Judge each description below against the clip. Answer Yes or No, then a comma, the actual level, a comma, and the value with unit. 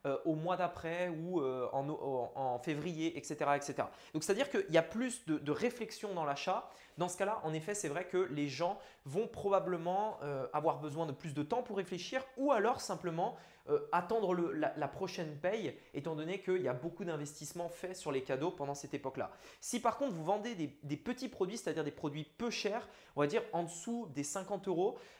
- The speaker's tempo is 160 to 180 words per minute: No, average, 200 wpm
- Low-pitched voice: No, medium, 175 Hz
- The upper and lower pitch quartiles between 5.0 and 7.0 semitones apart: Yes, wide, 5.4 semitones